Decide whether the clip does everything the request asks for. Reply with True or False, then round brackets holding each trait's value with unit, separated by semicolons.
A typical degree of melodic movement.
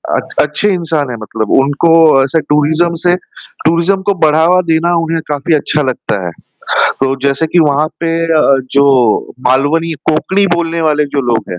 True (3.2 semitones)